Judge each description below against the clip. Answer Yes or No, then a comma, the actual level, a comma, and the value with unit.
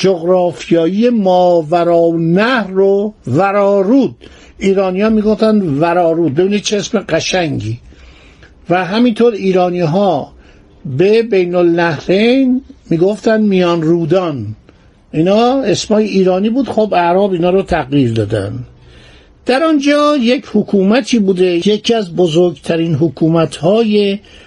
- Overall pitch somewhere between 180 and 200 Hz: Yes, medium, 185 Hz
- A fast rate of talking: No, average, 110 wpm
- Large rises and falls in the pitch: No, average, 4.1 semitones